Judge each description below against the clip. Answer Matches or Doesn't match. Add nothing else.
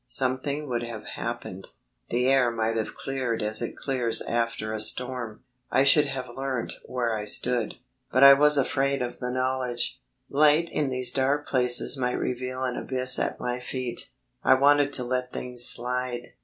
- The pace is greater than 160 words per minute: Matches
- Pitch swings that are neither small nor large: Doesn't match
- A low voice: Matches